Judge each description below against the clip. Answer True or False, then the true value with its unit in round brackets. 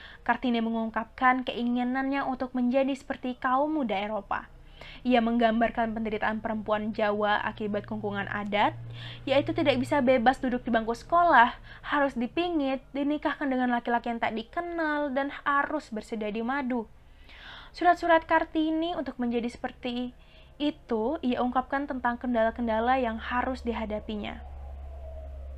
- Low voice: False (245 Hz)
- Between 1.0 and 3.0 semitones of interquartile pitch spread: False (3.8 semitones)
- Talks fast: False (120 wpm)